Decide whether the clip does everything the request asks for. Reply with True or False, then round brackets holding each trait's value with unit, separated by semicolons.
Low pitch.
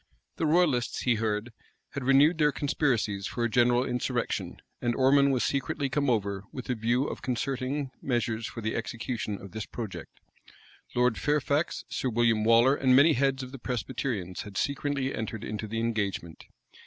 True (125 Hz)